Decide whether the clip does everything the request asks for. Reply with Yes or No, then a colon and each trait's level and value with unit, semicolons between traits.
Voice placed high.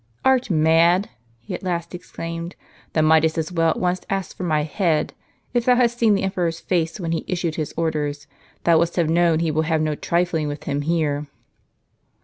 No: medium, 165 Hz